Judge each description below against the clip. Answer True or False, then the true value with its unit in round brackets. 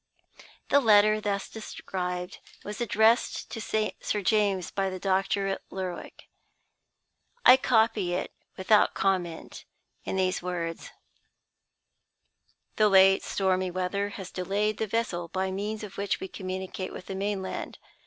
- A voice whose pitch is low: False (195 Hz)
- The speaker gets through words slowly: True (130 wpm)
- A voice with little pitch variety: True (2.2 semitones)